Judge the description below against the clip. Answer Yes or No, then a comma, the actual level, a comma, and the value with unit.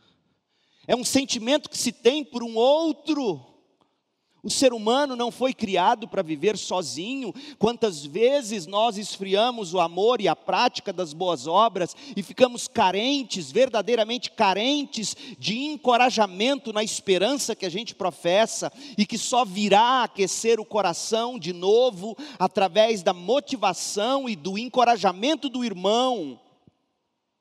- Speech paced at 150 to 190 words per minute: No, average, 130 wpm